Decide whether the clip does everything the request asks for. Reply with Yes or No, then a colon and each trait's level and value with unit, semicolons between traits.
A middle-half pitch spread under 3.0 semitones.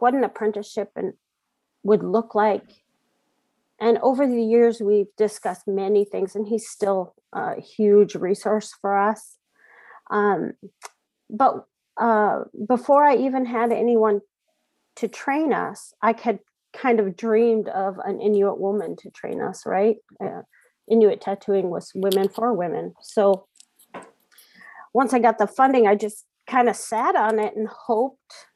Yes: narrow, 2.4 semitones